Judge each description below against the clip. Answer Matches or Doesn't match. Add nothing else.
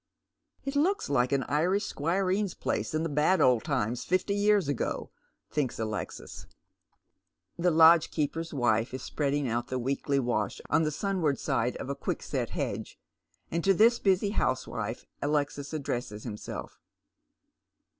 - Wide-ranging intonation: Matches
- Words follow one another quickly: Doesn't match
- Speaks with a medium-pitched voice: Matches